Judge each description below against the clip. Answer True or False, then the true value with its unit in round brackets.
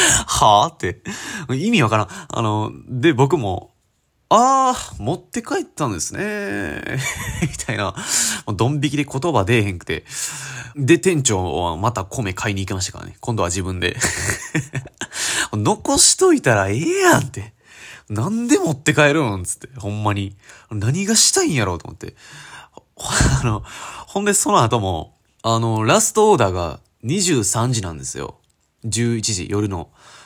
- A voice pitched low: True (115 Hz)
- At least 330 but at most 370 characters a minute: False (280 characters per minute)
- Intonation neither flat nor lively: False (8.9 semitones)